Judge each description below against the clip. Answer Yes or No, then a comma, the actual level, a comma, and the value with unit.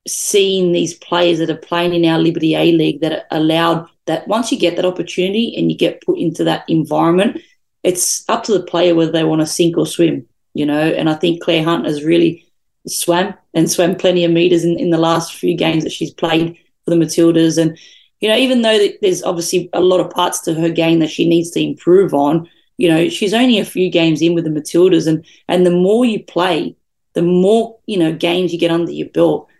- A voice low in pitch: No, medium, 170 Hz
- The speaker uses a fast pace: Yes, fast, 225 wpm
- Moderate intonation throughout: No, narrow, 1.8 semitones